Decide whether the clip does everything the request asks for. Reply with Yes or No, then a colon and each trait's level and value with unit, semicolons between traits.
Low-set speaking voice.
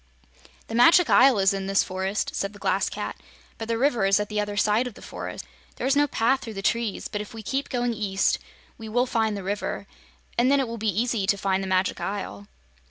No: high, 215 Hz